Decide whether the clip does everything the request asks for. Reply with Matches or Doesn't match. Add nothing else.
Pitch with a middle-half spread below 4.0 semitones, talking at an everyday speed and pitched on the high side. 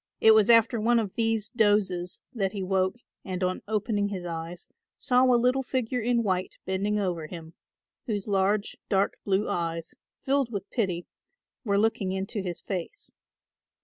Matches